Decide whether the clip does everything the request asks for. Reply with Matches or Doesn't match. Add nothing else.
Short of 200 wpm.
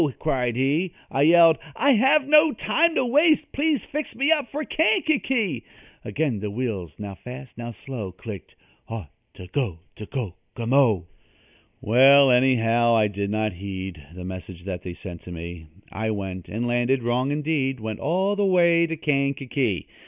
Matches